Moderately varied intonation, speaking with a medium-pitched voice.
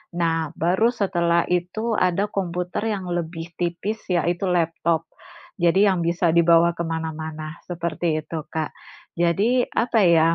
No: narrow, 1.9 semitones; medium, 170 Hz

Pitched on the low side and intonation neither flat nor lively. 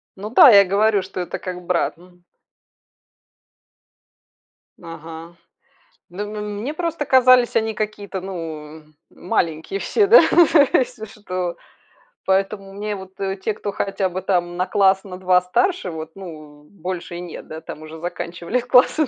No: high, 190 Hz; average, 3.3 semitones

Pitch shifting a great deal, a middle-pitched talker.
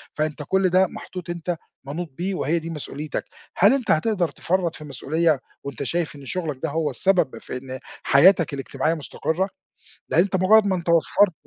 No: average, 3.8 semitones; medium, 165 Hz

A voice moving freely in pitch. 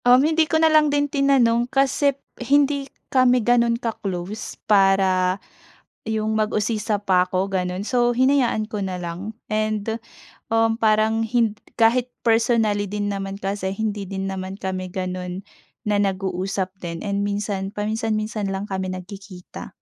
No: average, 3.4 semitones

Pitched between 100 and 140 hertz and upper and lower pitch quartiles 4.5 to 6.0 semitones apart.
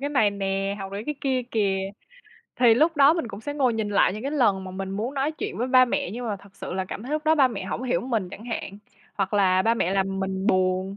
No: high, 210 Hz; average, 4.9 semitones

